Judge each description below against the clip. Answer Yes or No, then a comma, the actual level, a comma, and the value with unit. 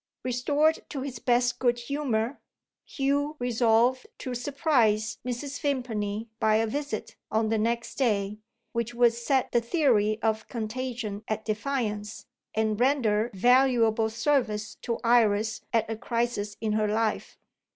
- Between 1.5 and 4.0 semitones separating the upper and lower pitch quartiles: Yes, average, 2.9 semitones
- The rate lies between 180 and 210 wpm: No, slow, 135 wpm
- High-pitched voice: Yes, high, 235 Hz